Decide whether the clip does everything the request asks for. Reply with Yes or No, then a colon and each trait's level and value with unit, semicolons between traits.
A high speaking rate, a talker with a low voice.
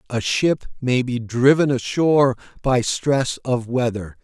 No: average, 140 wpm; low, 125 Hz